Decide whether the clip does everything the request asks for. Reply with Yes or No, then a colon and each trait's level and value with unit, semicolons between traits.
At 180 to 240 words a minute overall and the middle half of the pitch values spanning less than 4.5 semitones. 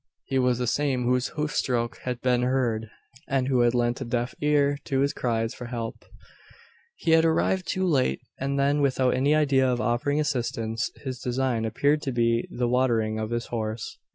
Yes: average, 185 wpm; average, 2.9 semitones